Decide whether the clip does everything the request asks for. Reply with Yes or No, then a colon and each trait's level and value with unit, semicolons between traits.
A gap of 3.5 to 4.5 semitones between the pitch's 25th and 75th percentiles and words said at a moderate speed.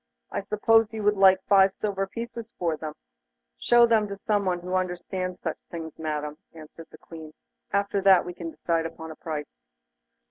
Yes: average, 3.9 semitones; average, 175 wpm